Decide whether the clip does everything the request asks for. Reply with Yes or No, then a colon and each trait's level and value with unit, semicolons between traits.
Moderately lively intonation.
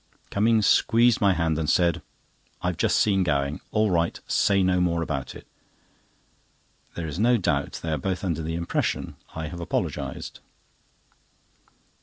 Yes: average, 3.6 semitones